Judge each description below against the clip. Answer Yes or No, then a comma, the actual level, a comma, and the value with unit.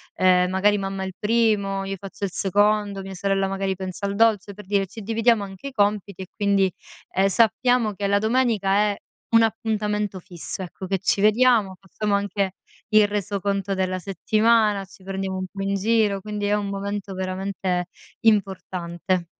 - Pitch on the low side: No, high, 200 Hz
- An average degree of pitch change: No, narrow, 1.6 semitones